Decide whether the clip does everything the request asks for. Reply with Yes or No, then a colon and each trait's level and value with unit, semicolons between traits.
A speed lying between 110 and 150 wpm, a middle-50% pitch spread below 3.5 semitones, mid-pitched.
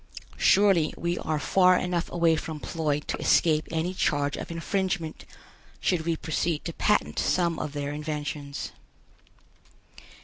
Yes: slow, 135 wpm; narrow, 2.6 semitones; medium, 165 Hz